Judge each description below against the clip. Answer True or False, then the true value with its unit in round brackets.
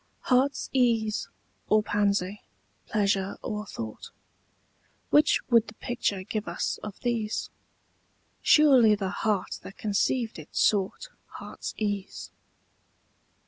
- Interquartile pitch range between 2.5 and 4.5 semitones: True (2.8 semitones)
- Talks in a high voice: True (215 Hz)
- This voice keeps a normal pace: False (105 wpm)